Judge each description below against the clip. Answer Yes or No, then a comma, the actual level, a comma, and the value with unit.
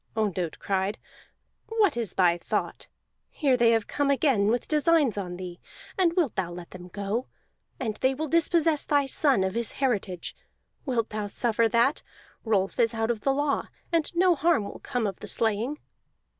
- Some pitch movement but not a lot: No, wide, 6.1 semitones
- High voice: Yes, high, 235 Hz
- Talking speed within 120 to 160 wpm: No, average, 175 wpm